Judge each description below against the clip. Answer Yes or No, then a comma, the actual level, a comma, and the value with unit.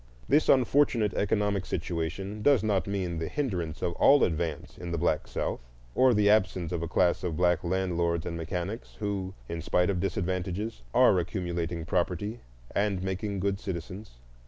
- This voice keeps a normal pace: Yes, average, 160 wpm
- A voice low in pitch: Yes, very low, 95 Hz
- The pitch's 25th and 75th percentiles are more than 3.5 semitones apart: No, average, 3.2 semitones